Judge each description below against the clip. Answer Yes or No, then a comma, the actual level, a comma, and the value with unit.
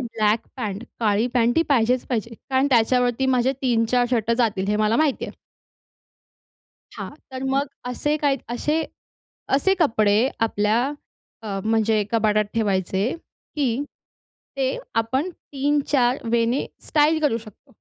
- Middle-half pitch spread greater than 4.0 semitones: No, average, 3.6 semitones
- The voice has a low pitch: No, high, 240 Hz